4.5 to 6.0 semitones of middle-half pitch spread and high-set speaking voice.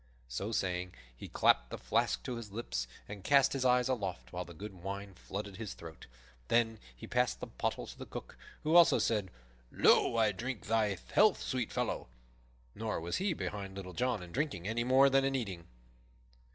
No: average, 5.2 semitones; low, 105 Hz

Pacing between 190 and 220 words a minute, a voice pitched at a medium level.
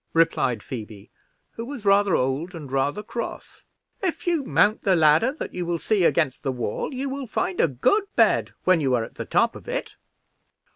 Yes: average, 195 wpm; medium, 175 Hz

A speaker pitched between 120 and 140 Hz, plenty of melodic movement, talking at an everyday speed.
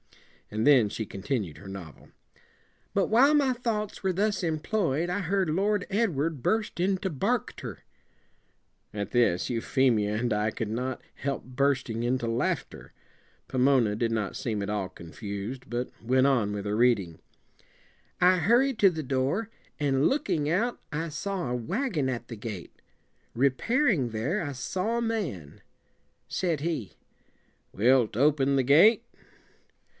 Yes: low, 135 Hz; wide, 8.8 semitones; average, 155 wpm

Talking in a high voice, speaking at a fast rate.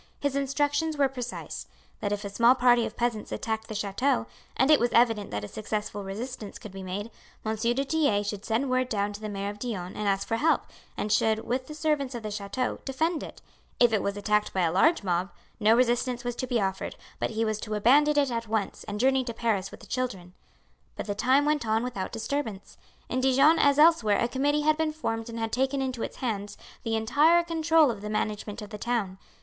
Yes: high, 230 Hz; fast, 225 wpm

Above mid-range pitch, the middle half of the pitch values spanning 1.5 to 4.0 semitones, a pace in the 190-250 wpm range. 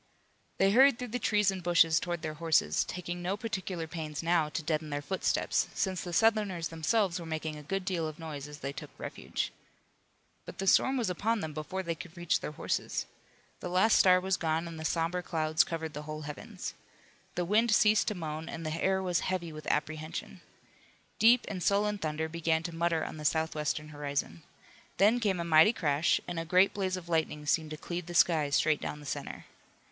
No: medium, 170 Hz; average, 3.3 semitones; fast, 205 wpm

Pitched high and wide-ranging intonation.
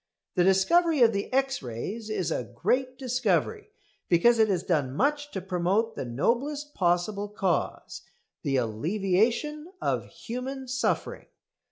Yes: high, 215 Hz; wide, 6.9 semitones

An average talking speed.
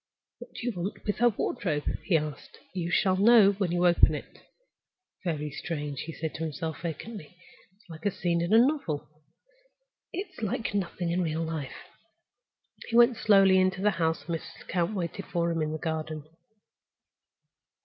Yes: average, 170 wpm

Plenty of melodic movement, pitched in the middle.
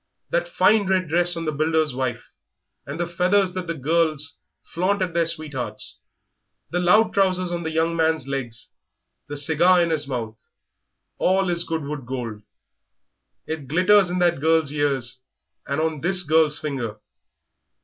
No: average, 3.9 semitones; medium, 160 Hz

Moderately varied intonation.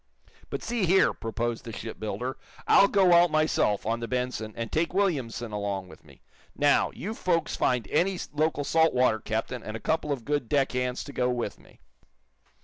No: wide, 5.9 semitones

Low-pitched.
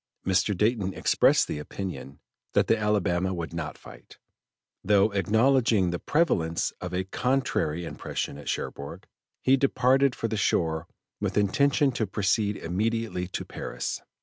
Yes: low, 100 Hz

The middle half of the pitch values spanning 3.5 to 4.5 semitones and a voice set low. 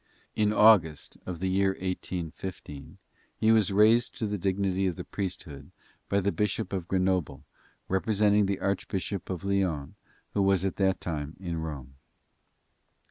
No: average, 2.8 semitones; very low, 95 Hz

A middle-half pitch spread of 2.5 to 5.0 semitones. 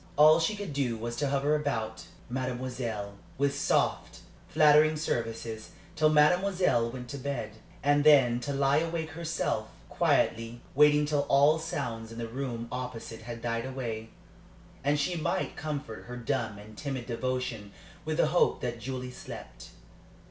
Yes: average, 4.2 semitones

